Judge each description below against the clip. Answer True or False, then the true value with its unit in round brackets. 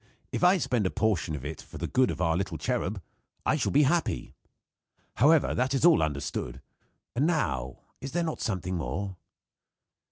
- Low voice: True (110 Hz)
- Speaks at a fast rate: False (180 wpm)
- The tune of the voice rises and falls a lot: True (8.9 semitones)